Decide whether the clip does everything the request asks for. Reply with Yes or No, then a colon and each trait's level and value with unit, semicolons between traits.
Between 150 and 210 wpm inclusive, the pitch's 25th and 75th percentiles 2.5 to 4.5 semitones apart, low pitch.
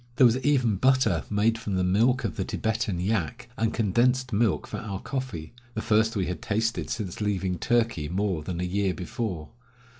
Yes: average, 185 wpm; average, 4.2 semitones; low, 105 Hz